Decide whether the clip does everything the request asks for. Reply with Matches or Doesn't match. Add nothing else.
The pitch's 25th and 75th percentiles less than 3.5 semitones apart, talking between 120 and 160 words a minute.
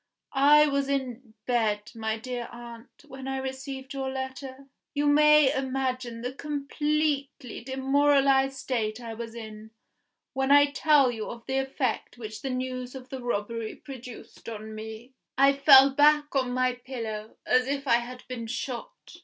Matches